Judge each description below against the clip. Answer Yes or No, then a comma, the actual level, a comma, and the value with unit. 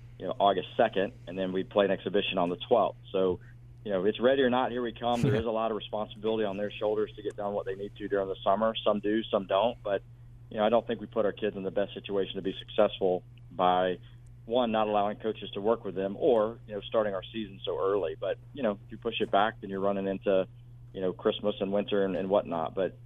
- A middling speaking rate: No, fast, 265 wpm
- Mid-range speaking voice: No, low, 105 Hz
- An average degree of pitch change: Yes, average, 3.3 semitones